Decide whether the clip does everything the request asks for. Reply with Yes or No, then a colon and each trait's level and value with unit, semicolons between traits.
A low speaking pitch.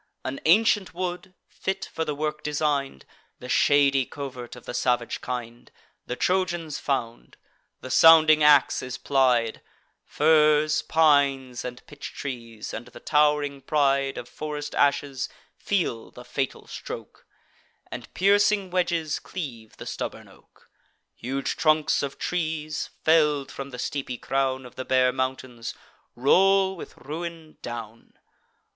No: medium, 145 Hz